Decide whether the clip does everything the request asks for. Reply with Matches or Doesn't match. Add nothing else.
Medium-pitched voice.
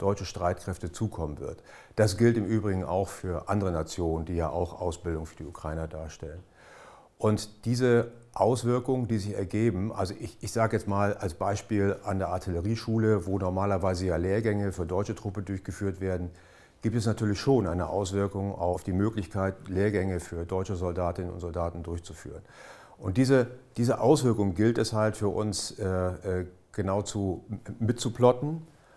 Doesn't match